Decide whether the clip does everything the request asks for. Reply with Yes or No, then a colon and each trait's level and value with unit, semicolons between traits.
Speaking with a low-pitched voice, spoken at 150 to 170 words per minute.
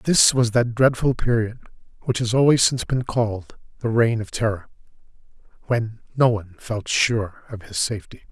Yes: low, 115 Hz; average, 165 wpm